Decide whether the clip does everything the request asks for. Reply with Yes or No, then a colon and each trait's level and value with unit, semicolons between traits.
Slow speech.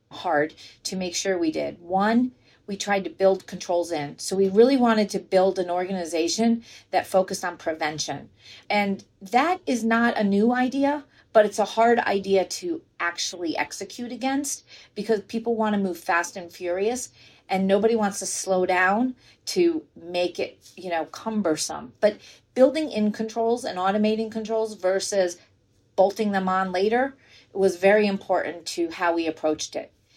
No: average, 165 wpm